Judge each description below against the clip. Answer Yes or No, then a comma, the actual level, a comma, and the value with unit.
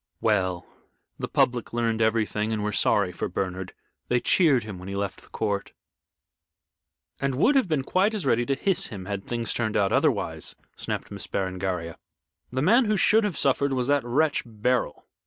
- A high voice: No, low, 115 Hz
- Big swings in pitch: Yes, wide, 5.9 semitones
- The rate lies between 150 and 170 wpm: No, average, 180 wpm